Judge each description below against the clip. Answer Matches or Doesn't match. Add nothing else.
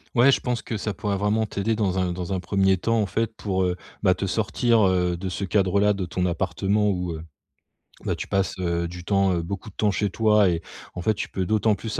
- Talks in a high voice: Doesn't match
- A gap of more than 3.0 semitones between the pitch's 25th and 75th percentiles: Doesn't match